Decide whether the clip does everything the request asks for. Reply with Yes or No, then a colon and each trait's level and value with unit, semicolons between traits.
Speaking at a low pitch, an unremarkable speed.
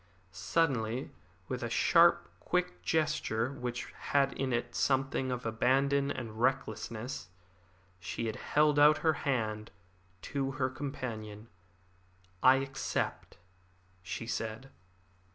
No: low, 130 Hz; slow, 105 wpm